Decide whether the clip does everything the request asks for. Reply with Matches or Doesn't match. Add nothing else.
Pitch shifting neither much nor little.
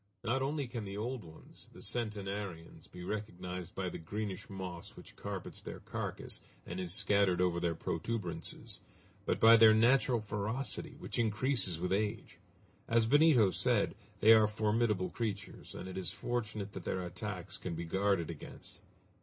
Matches